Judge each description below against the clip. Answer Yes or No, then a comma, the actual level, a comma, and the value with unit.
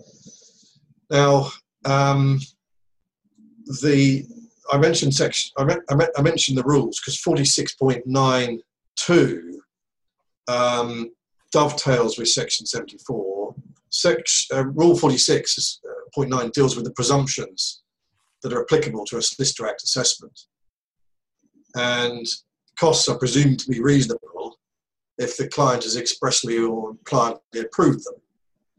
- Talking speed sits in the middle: No, slow, 110 wpm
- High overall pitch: No, low, 135 Hz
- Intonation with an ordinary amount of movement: Yes, average, 3.1 semitones